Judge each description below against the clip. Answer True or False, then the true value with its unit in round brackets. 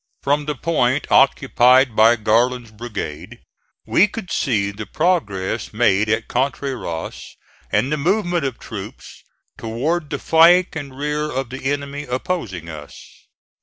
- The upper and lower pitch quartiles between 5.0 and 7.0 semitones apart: True (5.3 semitones)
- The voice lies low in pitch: True (130 Hz)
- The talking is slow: True (130 wpm)